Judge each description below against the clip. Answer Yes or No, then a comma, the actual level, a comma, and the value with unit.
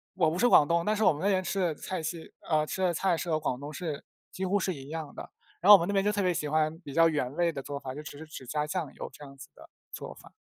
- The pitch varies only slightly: No, average, 3.8 semitones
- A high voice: No, medium, 160 Hz